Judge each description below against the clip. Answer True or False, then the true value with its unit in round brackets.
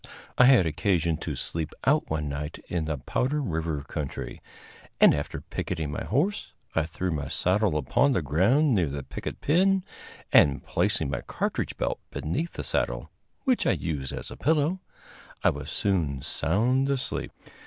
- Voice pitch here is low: True (85 Hz)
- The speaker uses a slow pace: False (165 wpm)